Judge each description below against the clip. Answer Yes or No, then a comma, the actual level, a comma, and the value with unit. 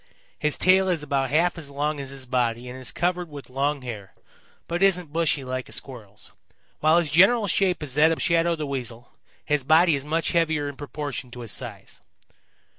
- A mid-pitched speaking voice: Yes, medium, 150 Hz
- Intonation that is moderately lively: Yes, average, 4.3 semitones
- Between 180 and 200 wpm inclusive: Yes, average, 195 wpm